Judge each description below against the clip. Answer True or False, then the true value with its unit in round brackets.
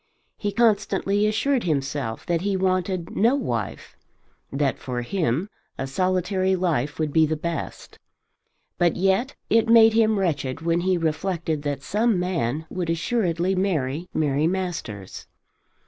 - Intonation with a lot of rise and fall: False (4.5 semitones)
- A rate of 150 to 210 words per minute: False (135 wpm)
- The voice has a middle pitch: True (175 Hz)